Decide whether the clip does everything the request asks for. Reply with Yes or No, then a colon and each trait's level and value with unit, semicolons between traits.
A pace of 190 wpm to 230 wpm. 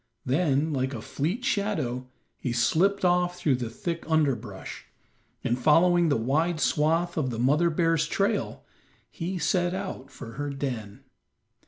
No: average, 145 wpm